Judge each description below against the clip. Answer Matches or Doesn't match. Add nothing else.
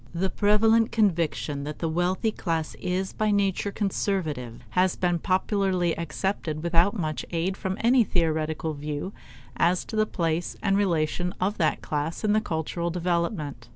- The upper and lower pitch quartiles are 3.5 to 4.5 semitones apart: Matches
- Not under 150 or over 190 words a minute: Matches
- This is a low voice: Doesn't match